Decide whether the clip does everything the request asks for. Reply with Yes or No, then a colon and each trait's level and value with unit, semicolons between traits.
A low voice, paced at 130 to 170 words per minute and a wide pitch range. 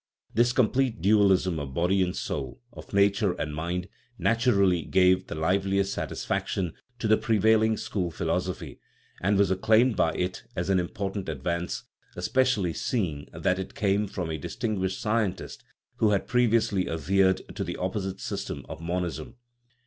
No: very low, 95 Hz; average, 155 wpm; average, 3.3 semitones